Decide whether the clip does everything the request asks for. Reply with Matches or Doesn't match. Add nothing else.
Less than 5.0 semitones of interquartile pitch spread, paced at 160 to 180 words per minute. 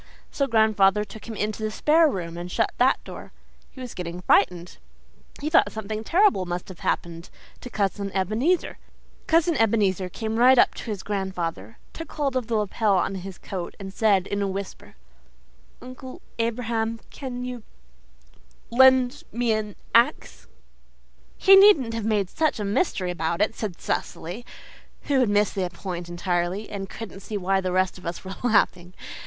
Matches